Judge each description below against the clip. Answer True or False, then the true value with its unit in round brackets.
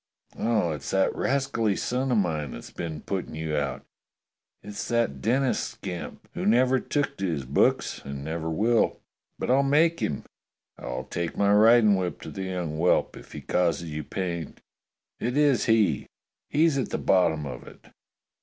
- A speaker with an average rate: True (170 wpm)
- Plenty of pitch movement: True (7.2 semitones)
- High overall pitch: False (95 Hz)